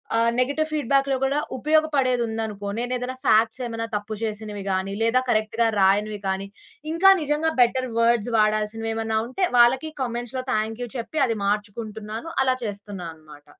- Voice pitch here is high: Yes, high, 225 Hz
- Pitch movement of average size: Yes, average, 3.3 semitones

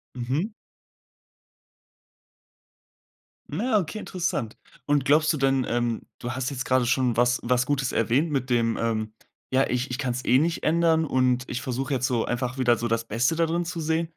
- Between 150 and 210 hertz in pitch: No, low, 130 Hz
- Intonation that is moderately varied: Yes, average, 4.1 semitones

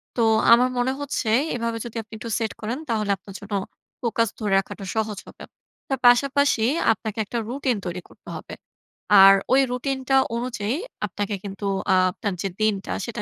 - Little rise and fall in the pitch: No, average, 3.3 semitones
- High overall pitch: Yes, high, 230 Hz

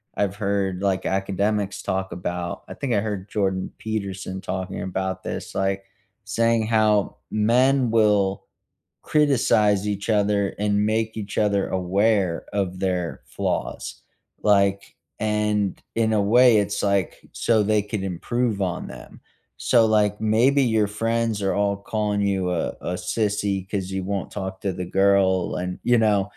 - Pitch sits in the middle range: No, low, 100 Hz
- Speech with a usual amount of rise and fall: No, narrow, 2.1 semitones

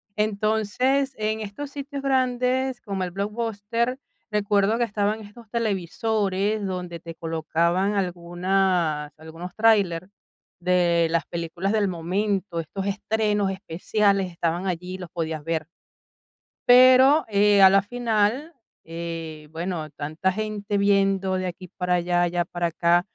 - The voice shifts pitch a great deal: No, average, 3.8 semitones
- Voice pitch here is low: No, high, 195 Hz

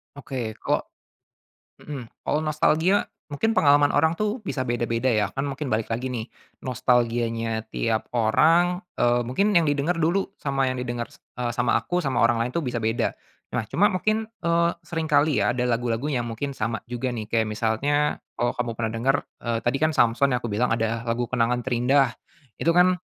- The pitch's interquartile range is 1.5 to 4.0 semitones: No, average, 4.6 semitones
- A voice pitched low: Yes, low, 125 Hz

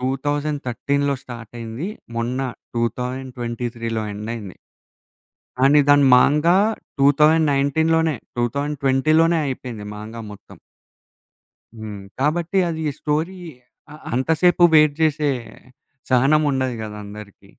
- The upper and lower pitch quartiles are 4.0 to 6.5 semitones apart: Yes, average, 4.4 semitones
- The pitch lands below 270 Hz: Yes, low, 135 Hz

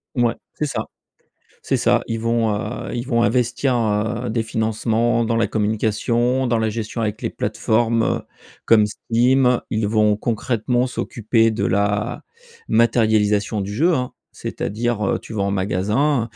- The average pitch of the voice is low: Yes, low, 115 Hz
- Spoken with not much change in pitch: Yes, narrow, 2.0 semitones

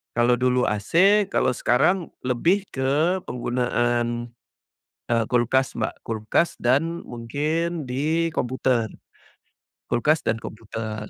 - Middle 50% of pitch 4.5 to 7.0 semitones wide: Yes, average, 5.1 semitones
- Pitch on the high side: No, low, 125 Hz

